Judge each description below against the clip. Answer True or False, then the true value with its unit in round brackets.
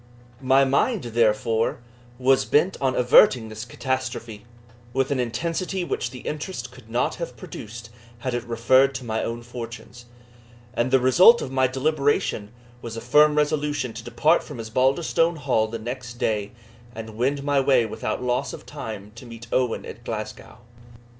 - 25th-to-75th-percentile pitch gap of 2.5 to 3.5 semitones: True (3.1 semitones)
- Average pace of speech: True (160 wpm)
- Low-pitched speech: True (125 Hz)